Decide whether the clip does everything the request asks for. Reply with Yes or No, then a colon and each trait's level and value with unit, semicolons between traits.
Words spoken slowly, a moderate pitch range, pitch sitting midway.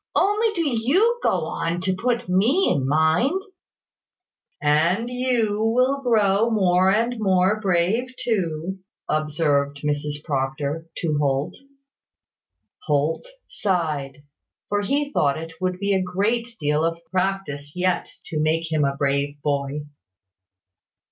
No: slow, 130 wpm; wide, 7.0 semitones; medium, 180 Hz